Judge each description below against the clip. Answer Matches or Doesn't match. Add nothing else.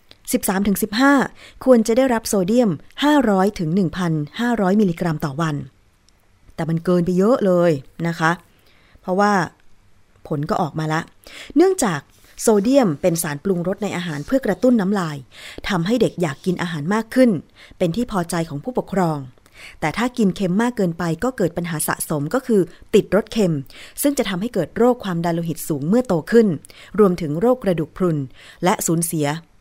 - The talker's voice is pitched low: Doesn't match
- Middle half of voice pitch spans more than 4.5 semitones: Matches